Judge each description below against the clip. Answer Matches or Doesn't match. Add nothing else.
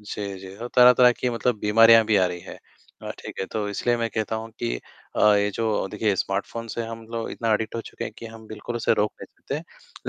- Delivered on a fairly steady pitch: Matches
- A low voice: Matches